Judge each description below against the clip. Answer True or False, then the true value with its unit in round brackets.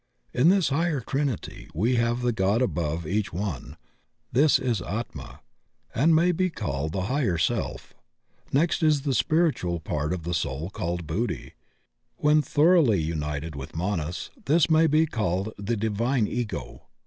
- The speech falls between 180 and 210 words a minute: False (150 wpm)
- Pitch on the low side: True (110 Hz)